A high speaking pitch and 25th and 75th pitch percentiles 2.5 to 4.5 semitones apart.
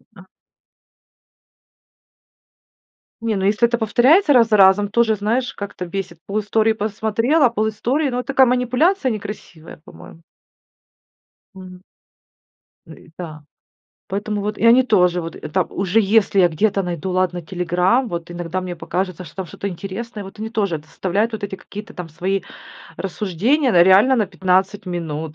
Yes: high, 200 Hz; average, 3.7 semitones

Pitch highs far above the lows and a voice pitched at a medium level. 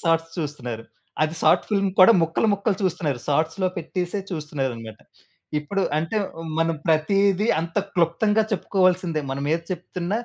No: average, 3.5 semitones; medium, 165 Hz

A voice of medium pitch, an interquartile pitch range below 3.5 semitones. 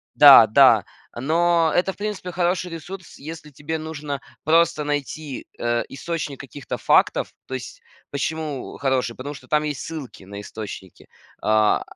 No: medium, 150 Hz; average, 4.0 semitones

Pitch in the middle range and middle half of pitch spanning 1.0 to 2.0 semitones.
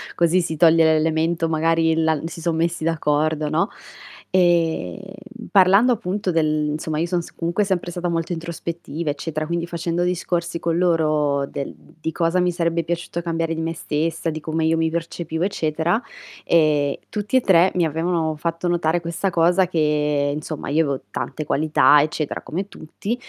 Yes: medium, 165 Hz; narrow, 1.6 semitones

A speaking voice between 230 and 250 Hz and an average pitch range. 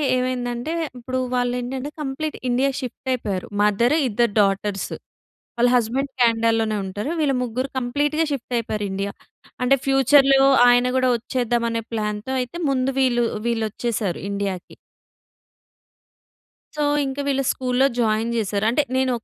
Yes: high, 245 Hz; average, 3.2 semitones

